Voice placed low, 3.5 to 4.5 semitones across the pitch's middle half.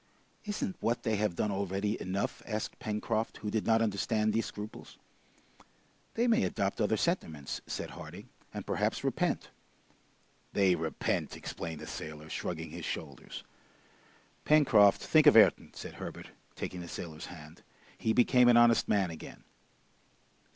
No: low, 105 Hz; average, 4.9 semitones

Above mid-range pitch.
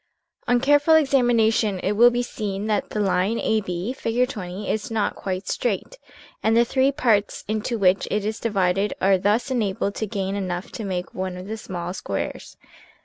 Yes: high, 210 Hz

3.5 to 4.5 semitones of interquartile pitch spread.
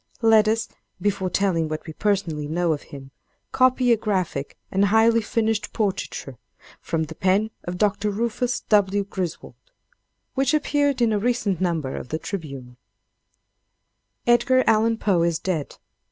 No: average, 5.1 semitones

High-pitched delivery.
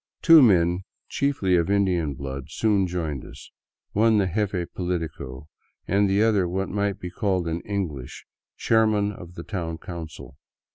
No: very low, 90 Hz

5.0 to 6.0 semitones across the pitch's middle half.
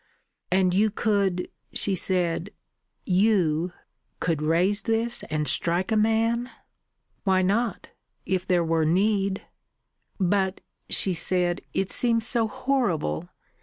No: average, 3.8 semitones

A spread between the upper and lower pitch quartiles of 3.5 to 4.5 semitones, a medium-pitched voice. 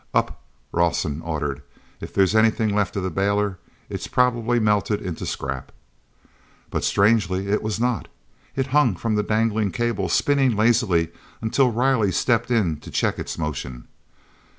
No: average, 4.0 semitones; low, 105 Hz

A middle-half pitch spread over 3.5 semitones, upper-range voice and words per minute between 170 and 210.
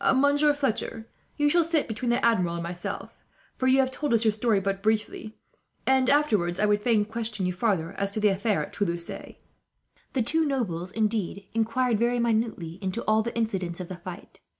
Yes: average, 4.2 semitones; high, 220 Hz; average, 195 wpm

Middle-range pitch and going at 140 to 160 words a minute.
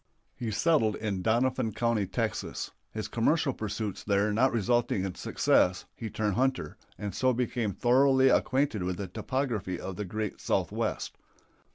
No: low, 110 Hz; average, 150 wpm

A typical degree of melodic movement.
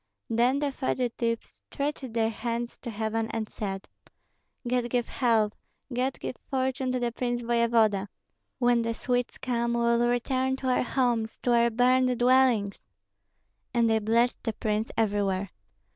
No: narrow, 2.0 semitones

